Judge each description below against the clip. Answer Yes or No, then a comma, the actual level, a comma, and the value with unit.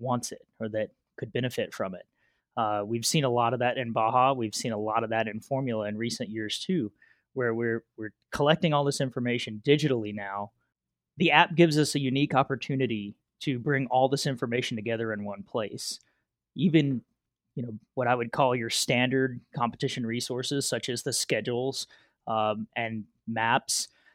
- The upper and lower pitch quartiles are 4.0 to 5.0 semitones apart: No, average, 3.3 semitones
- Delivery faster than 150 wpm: Yes, average, 180 wpm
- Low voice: Yes, low, 120 Hz